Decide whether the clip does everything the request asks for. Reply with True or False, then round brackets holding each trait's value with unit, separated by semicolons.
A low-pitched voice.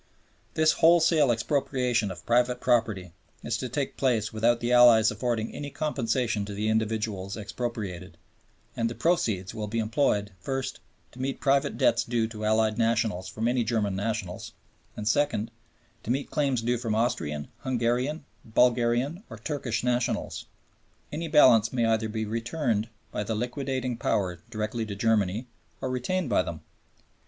True (115 Hz)